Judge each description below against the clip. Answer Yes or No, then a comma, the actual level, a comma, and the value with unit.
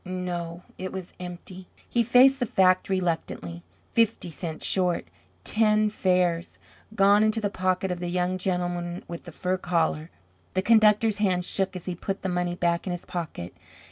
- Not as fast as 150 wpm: No, average, 170 wpm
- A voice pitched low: No, medium, 185 Hz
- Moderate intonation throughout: No, narrow, 2.1 semitones